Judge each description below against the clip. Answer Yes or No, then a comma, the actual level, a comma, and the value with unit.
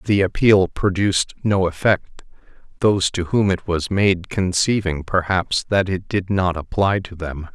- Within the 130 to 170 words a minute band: Yes, average, 160 wpm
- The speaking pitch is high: No, very low, 95 Hz